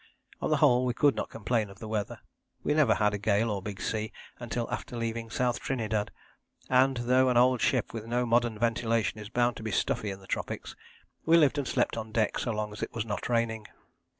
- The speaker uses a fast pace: Yes, fast, 225 wpm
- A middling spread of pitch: No, narrow, 2.3 semitones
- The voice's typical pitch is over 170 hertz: No, low, 115 Hz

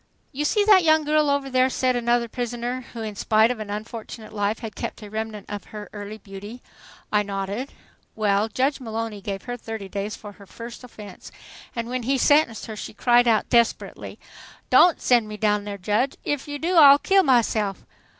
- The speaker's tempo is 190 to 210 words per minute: Yes, average, 195 wpm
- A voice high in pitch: Yes, high, 230 Hz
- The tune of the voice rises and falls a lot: No, average, 3.6 semitones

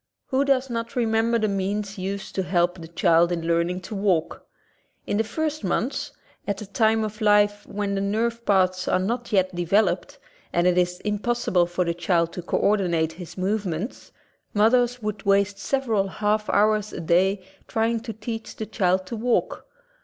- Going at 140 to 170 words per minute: No, average, 185 wpm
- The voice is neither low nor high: No, high, 200 Hz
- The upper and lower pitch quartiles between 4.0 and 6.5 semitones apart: No, average, 3.4 semitones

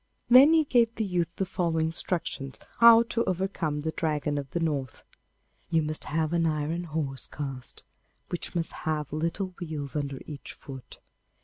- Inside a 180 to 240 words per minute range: No, average, 165 wpm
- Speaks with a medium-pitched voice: Yes, medium, 160 Hz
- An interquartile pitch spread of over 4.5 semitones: No, average, 3.6 semitones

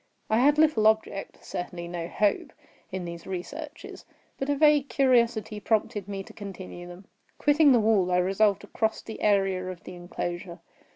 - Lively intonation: No, average, 4.8 semitones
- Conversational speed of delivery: Yes, average, 160 wpm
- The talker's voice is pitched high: Yes, high, 205 Hz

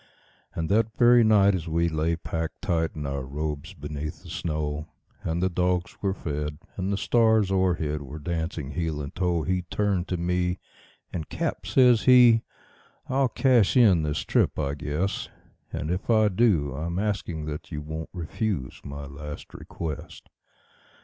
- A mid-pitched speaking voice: No, very low, 85 Hz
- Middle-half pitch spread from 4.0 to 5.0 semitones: Yes, average, 4.6 semitones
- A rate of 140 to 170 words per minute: Yes, average, 165 wpm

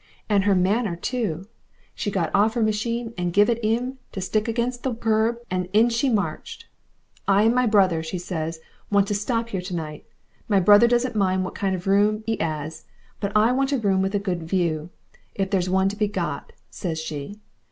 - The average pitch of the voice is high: Yes, high, 200 Hz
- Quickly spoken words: Yes, fast, 210 wpm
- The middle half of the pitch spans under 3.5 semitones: No, average, 3.8 semitones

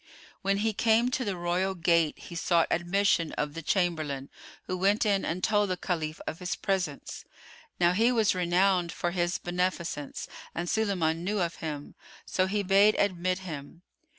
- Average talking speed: Yes, average, 175 wpm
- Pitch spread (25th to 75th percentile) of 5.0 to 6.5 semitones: No, average, 2.8 semitones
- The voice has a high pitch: No, medium, 180 Hz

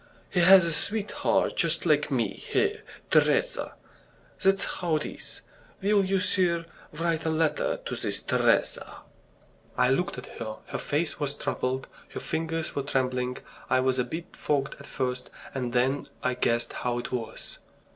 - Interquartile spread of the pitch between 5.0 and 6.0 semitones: Yes, average, 5.3 semitones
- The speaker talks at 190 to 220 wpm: No, average, 160 wpm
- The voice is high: No, medium, 150 Hz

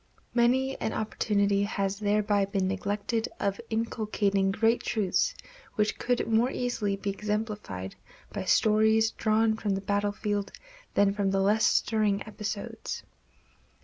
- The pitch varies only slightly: Yes, narrow, 1.7 semitones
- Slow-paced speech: Yes, slow, 120 wpm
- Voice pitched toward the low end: No, high, 210 Hz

